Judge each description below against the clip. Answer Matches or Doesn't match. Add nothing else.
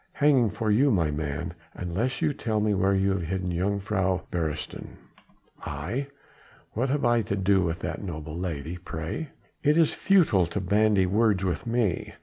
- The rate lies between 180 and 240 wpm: Doesn't match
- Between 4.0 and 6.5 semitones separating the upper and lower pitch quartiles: Matches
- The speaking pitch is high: Doesn't match